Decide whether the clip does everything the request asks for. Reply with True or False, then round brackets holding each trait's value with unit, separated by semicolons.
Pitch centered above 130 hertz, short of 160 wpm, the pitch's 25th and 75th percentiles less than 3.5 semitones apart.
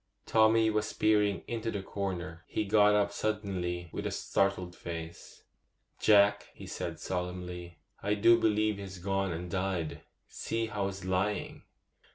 False (100 Hz; 145 wpm; 2.9 semitones)